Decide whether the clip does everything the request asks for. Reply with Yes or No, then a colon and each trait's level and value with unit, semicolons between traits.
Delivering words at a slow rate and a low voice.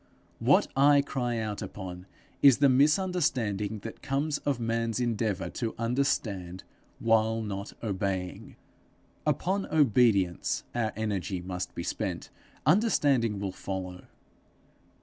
Yes: slow, 110 wpm; low, 115 Hz